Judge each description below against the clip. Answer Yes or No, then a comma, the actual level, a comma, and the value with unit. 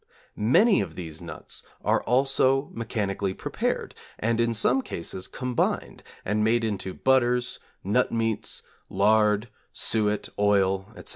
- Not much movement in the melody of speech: No, average, 3.7 semitones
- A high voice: No, low, 110 Hz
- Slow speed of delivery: Yes, slow, 125 wpm